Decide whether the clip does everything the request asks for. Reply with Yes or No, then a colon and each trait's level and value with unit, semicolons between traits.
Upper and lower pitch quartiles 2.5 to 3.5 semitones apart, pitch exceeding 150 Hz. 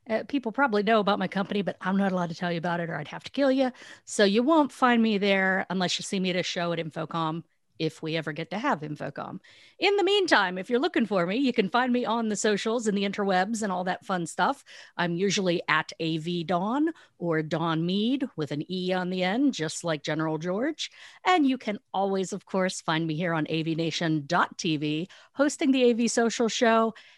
No: wide, 5.6 semitones; high, 190 Hz